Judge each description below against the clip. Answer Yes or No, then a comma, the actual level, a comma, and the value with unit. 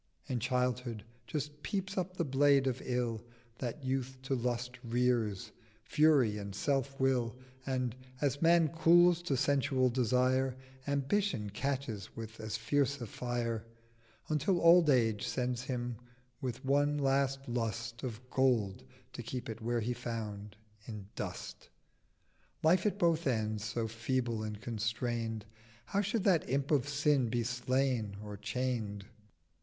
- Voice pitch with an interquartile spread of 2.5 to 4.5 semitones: Yes, average, 3.6 semitones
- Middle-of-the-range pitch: No, low, 125 Hz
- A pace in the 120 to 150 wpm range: Yes, average, 140 wpm